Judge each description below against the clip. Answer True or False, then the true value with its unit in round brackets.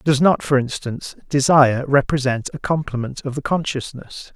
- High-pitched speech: False (140 Hz)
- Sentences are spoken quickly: False (150 wpm)